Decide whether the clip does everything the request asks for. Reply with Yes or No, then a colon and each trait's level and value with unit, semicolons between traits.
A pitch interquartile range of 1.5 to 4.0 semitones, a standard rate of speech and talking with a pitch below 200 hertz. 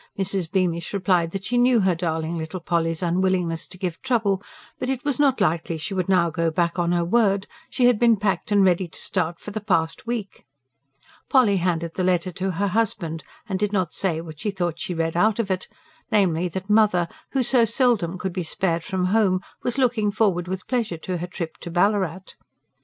No: average, 3.6 semitones; fast, 210 wpm; medium, 185 Hz